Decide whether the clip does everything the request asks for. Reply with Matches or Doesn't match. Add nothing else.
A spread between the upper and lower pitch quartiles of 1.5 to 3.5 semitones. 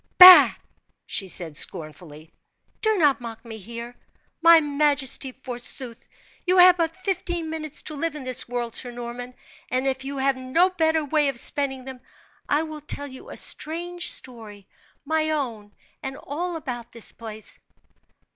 Doesn't match